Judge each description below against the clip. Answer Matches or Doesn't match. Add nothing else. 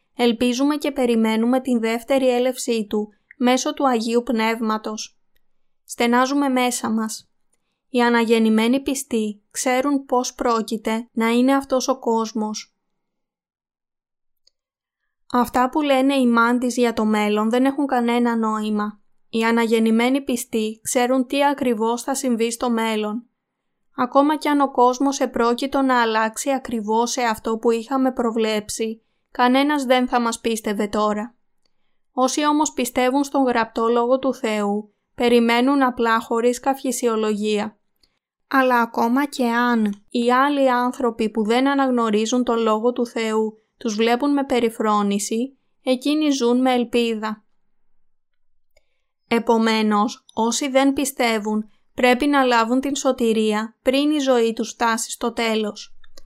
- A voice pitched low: Doesn't match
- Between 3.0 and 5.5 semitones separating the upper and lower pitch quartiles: Doesn't match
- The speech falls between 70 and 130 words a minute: Matches